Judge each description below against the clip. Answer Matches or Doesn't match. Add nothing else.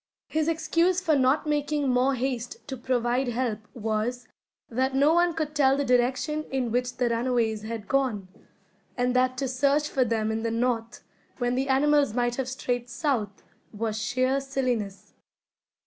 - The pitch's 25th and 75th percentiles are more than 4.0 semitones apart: Doesn't match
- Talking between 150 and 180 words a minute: Matches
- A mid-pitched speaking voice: Doesn't match